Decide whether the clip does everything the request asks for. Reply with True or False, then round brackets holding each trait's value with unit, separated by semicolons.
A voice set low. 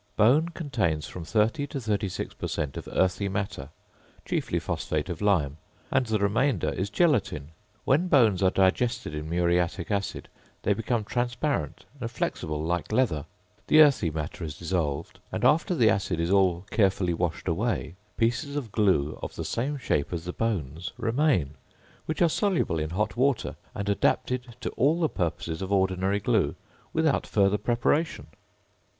True (100 Hz)